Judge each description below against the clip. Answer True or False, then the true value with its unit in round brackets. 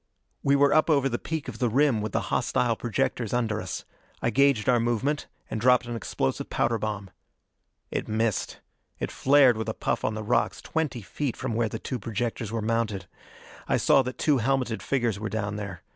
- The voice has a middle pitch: False (115 Hz)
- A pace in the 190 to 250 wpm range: True (200 wpm)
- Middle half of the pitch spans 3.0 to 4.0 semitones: True (3.7 semitones)